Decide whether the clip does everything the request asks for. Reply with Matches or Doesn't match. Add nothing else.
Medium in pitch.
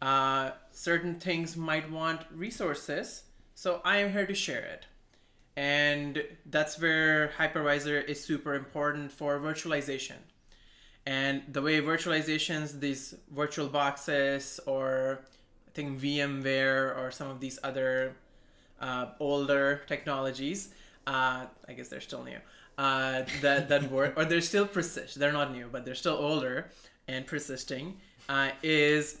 Matches